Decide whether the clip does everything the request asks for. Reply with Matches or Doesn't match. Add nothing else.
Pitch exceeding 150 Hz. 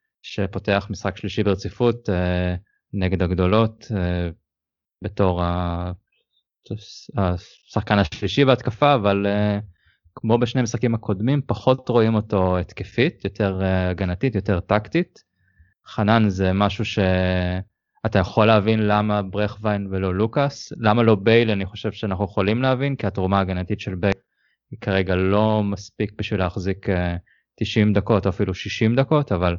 Doesn't match